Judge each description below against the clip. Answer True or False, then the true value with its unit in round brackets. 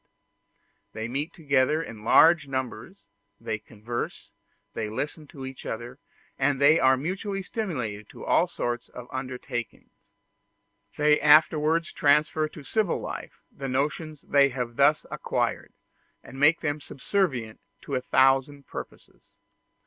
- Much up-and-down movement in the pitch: False (3.5 semitones)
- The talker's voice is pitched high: False (140 Hz)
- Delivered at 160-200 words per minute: False (135 wpm)